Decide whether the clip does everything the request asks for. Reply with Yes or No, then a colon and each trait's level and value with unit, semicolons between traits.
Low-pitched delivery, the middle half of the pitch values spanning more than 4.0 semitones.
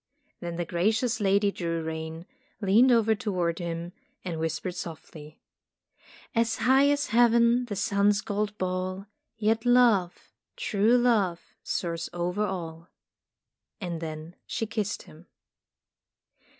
No: high, 195 Hz; average, 4.7 semitones